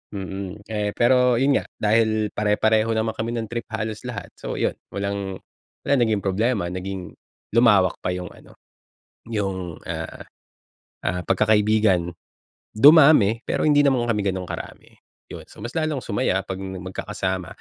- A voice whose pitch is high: No, low, 105 Hz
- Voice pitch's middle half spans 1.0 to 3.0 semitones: No, average, 3.4 semitones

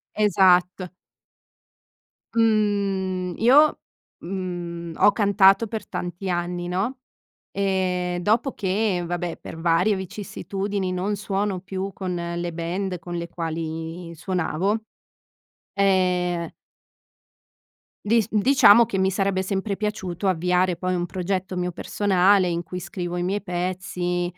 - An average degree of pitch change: No, narrow, 2.2 semitones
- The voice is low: No, medium, 185 Hz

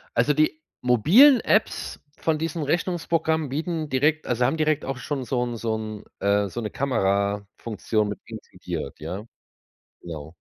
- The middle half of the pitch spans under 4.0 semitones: No, wide, 6.8 semitones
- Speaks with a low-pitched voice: Yes, low, 130 Hz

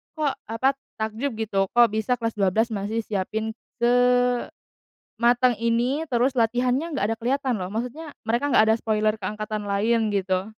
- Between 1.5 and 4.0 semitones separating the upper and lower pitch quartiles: Yes, average, 2.7 semitones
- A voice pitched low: No, high, 225 Hz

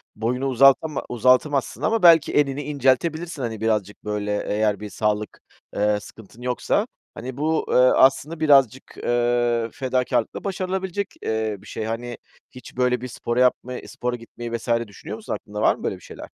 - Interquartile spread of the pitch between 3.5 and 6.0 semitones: Yes, average, 3.8 semitones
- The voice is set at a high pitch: No, low, 125 Hz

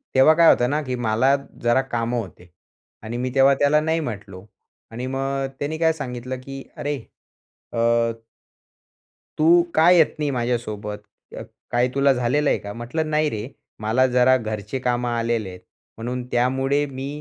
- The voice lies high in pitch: No, low, 125 Hz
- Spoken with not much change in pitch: No, average, 3.3 semitones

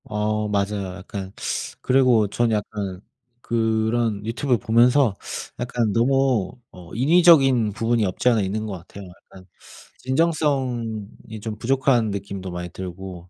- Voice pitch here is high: No, low, 110 Hz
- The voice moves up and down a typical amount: Yes, average, 3.8 semitones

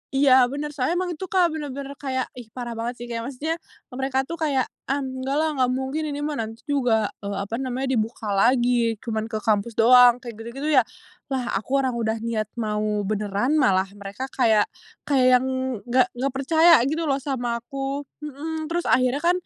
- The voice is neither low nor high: No, very high, 255 Hz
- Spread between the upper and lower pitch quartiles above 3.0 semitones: Yes, average, 3.5 semitones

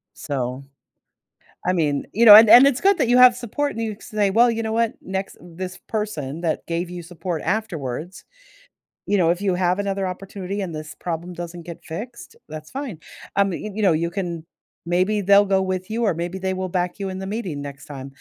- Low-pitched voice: No, medium, 185 Hz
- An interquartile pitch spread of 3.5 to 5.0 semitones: Yes, average, 3.9 semitones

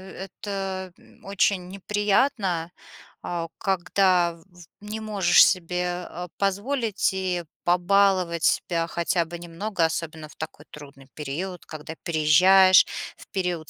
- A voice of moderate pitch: Yes, medium, 180 Hz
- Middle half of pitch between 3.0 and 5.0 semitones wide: No, narrow, 2.6 semitones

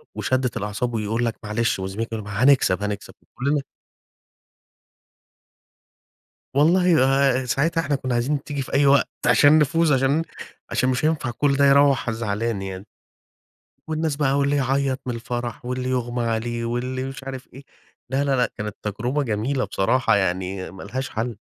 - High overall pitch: No, low, 130 Hz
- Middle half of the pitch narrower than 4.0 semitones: Yes, average, 3.6 semitones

